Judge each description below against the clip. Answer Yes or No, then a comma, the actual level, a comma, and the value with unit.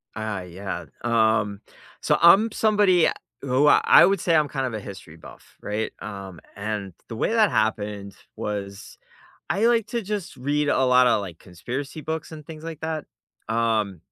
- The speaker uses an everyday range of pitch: No, wide, 7.7 semitones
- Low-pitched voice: Yes, low, 125 Hz